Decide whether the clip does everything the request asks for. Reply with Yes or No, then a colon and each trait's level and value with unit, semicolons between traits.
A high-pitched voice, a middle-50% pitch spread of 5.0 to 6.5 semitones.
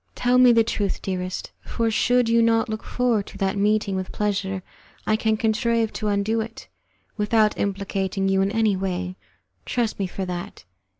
No: high, 210 Hz; average, 2.8 semitones